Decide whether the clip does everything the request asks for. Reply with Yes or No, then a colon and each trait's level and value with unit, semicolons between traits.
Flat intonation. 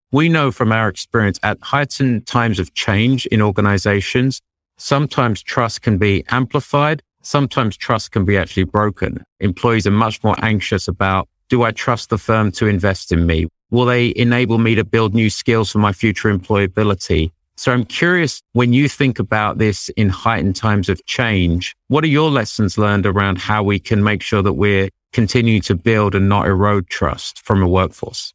No: average, 3.5 semitones